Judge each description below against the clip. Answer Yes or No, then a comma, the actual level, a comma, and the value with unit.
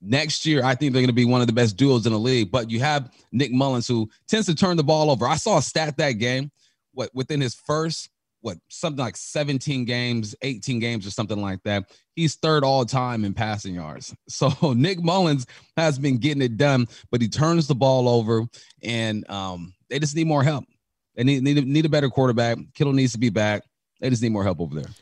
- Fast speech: Yes, fast, 235 wpm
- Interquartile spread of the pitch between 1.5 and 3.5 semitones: No, average, 4.1 semitones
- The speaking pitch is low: Yes, low, 130 Hz